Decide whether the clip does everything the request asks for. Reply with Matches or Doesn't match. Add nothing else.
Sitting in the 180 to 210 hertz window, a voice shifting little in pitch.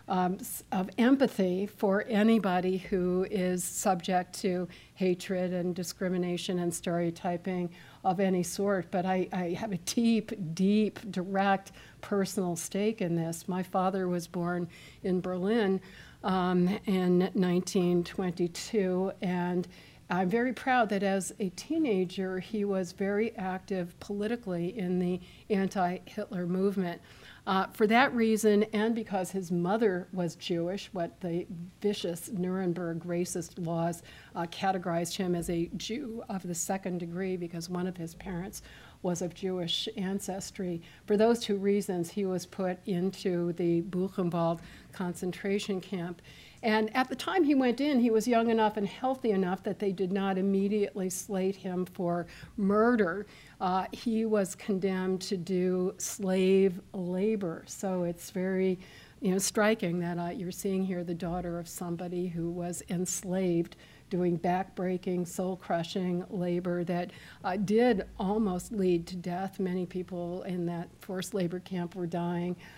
Matches